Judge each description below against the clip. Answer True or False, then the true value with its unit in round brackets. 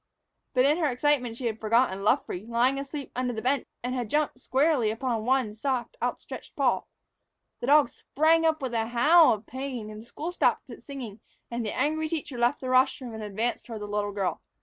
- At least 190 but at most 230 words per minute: True (200 wpm)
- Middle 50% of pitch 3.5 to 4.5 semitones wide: True (4.0 semitones)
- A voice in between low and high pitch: False (250 Hz)